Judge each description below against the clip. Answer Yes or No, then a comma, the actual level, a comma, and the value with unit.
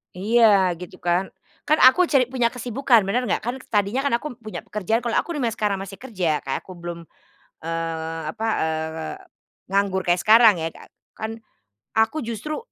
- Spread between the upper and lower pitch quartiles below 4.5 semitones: No, average, 5.3 semitones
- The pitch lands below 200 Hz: No, high, 215 Hz